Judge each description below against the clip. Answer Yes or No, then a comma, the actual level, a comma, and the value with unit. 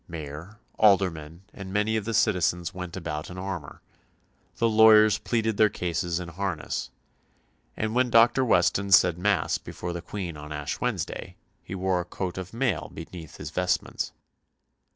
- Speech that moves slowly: No, average, 155 wpm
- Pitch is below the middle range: Yes, very low, 95 Hz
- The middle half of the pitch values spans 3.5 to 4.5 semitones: Yes, average, 4.0 semitones